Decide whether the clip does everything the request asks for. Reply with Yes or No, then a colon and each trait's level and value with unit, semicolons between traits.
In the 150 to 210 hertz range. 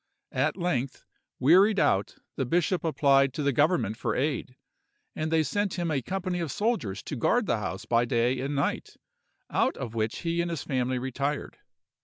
No: medium, 140 Hz